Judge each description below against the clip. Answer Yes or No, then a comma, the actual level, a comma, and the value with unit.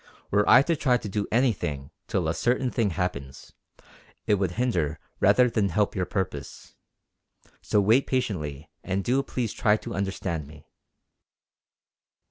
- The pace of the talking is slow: No, average, 145 wpm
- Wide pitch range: Yes, wide, 6.2 semitones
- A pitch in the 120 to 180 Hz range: No, low, 100 Hz